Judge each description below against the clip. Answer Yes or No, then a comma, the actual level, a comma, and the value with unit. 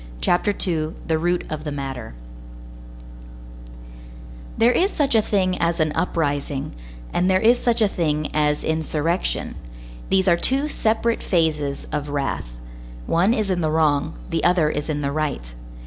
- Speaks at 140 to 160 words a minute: Yes, average, 150 wpm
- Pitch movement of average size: Yes, average, 4.2 semitones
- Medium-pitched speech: Yes, medium, 160 Hz